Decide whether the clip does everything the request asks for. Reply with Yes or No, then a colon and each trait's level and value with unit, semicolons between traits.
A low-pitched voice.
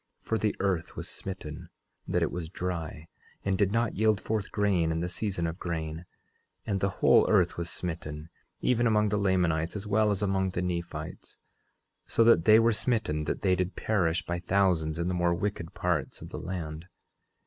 Yes: very low, 90 Hz